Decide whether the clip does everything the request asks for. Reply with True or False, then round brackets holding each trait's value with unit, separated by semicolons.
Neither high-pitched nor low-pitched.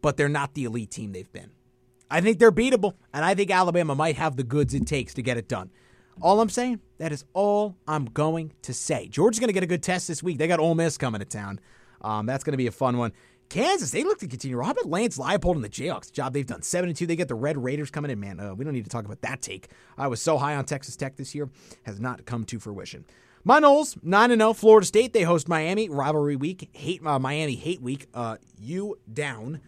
True (150 Hz)